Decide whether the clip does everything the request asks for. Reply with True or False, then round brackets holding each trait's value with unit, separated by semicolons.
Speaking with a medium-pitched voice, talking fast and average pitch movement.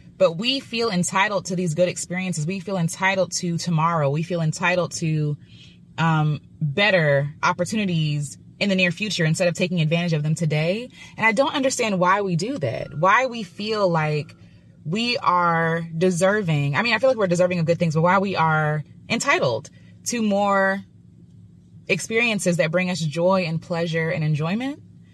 False (180 Hz; 170 wpm; 3.3 semitones)